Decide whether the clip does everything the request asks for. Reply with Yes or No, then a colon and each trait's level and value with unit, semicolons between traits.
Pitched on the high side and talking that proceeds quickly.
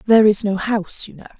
Yes: high, 205 Hz; fast, 260 wpm